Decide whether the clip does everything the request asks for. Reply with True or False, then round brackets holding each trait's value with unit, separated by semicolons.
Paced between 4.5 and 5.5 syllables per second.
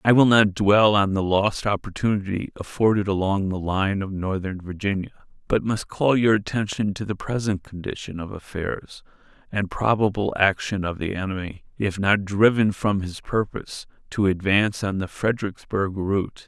True (4.9 syllables/s)